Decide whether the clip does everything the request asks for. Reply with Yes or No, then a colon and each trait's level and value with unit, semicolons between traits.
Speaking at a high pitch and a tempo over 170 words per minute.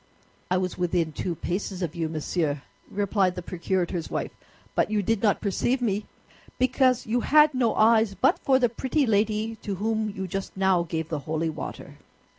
Yes: high, 195 Hz; average, 180 wpm